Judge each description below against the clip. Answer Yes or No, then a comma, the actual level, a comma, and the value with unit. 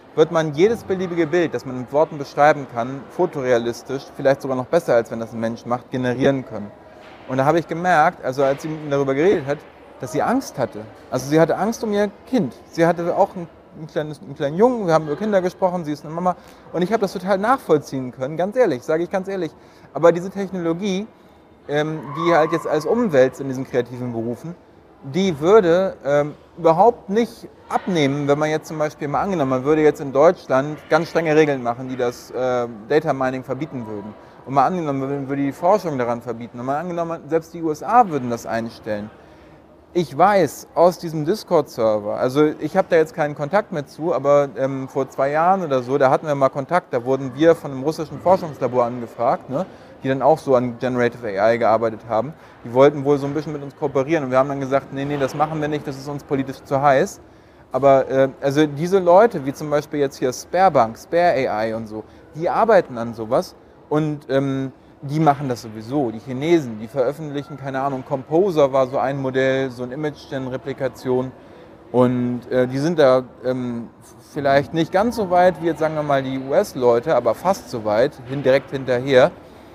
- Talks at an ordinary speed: No, fast, 205 wpm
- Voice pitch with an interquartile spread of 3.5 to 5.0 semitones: Yes, average, 4.1 semitones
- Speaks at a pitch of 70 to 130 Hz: No, medium, 140 Hz